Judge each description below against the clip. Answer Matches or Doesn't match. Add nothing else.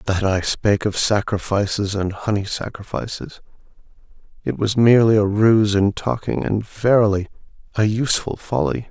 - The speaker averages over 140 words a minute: Doesn't match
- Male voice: Matches